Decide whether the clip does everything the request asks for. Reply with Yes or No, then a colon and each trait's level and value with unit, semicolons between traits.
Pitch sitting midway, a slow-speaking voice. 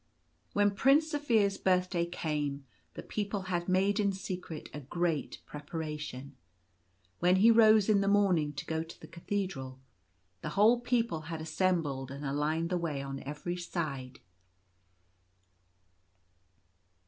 Yes: medium, 175 Hz; slow, 130 wpm